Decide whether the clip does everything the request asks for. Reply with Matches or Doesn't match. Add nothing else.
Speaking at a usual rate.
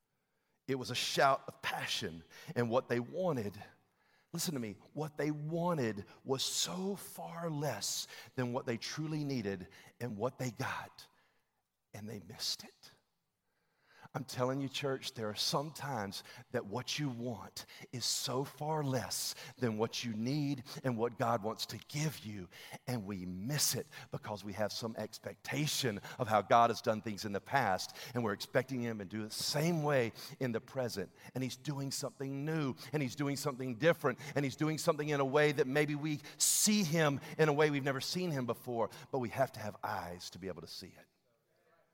Matches